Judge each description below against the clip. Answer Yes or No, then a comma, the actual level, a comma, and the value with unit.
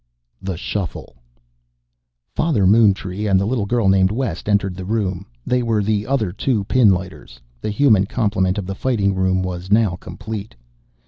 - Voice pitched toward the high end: No, low, 100 Hz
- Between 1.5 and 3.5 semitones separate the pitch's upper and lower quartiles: Yes, average, 2.9 semitones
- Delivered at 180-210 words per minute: No, average, 155 wpm